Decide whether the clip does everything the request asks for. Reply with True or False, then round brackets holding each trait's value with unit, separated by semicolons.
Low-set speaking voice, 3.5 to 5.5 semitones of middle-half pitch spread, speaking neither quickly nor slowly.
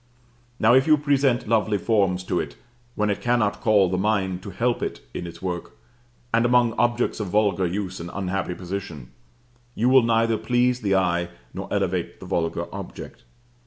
True (105 Hz; 4.4 semitones; 175 wpm)